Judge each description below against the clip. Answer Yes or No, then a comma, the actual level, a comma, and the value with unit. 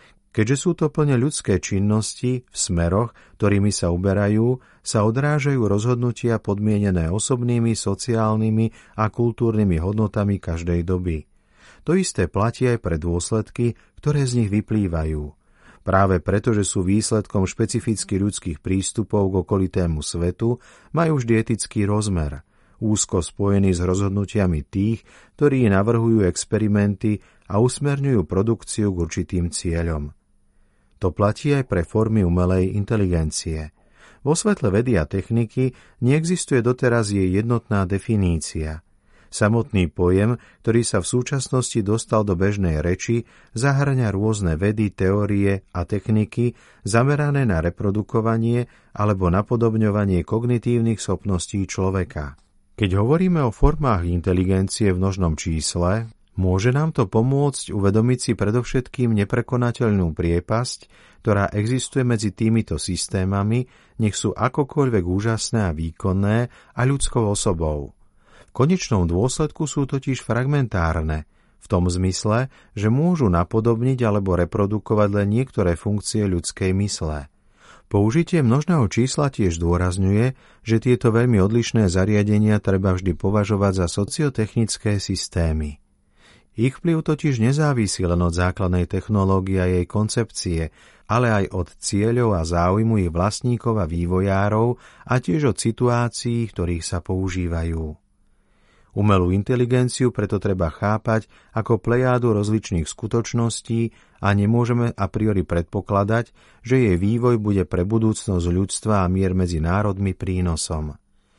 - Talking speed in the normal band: Yes, average, 120 wpm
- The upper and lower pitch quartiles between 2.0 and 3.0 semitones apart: No, average, 4.2 semitones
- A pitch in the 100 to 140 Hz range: Yes, low, 105 Hz